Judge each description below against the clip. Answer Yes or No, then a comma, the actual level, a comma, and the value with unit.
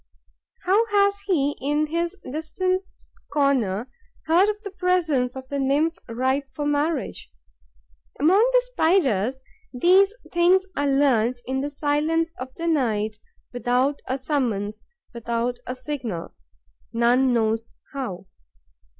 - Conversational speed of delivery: No, slow, 125 wpm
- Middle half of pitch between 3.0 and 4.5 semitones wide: No, average, 5.3 semitones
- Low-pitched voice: No, very high, 280 Hz